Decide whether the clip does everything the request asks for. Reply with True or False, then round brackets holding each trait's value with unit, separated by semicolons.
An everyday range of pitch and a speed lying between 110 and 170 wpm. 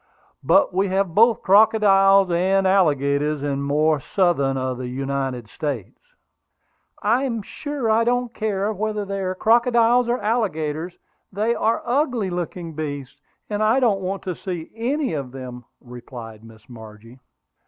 False (7.7 semitones; 150 wpm)